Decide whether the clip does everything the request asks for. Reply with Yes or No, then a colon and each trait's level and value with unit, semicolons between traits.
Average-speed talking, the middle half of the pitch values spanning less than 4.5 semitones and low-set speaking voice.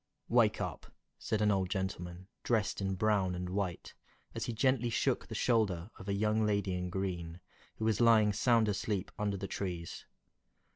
Yes: average, 175 wpm; average, 2.9 semitones; low, 100 Hz